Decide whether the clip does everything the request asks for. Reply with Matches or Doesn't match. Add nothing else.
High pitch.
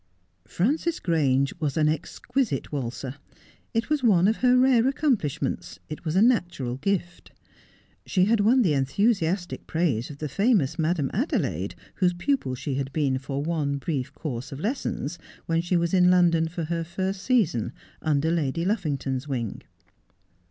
Doesn't match